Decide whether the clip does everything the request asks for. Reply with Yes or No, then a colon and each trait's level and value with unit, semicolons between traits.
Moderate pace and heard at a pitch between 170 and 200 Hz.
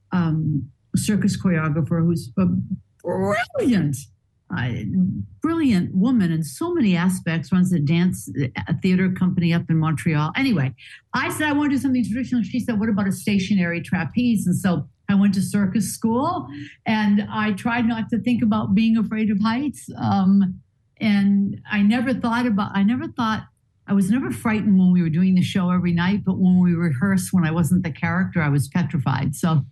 Yes: average, 180 wpm; high, 190 Hz